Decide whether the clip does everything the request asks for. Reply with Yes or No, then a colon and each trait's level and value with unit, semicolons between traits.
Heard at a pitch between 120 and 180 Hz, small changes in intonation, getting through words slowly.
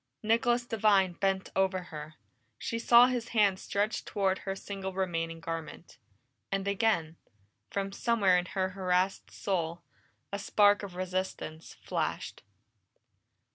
No: high, 190 Hz; narrow, 2.3 semitones; slow, 125 wpm